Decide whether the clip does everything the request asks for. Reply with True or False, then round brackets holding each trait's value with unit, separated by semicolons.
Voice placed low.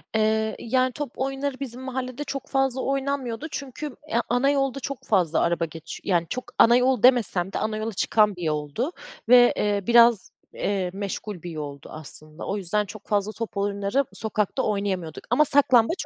False (220 Hz)